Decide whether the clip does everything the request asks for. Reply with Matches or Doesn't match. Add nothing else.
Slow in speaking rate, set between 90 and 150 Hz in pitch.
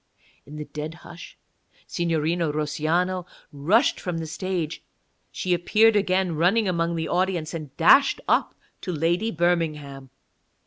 Doesn't match